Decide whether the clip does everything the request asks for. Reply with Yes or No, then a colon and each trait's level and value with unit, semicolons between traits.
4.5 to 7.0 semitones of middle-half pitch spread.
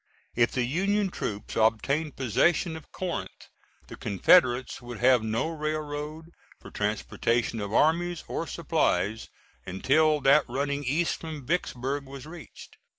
Yes: average, 4.9 semitones